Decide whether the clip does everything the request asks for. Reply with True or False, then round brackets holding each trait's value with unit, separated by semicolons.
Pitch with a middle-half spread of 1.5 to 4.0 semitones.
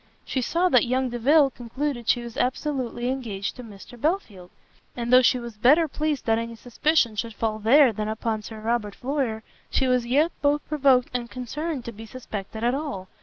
True (3.6 semitones)